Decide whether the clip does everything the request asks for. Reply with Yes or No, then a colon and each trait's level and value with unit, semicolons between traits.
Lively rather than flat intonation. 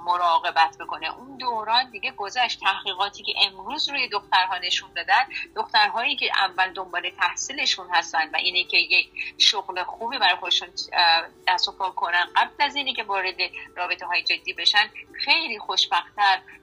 No: average, 4.4 semitones